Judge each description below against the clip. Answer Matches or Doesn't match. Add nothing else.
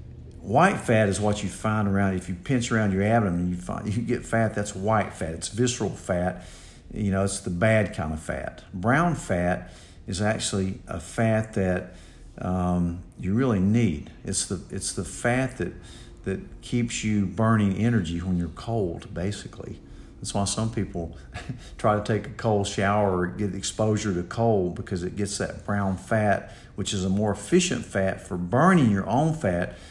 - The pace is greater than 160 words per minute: Matches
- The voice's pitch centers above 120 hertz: Doesn't match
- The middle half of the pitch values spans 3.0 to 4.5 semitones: Matches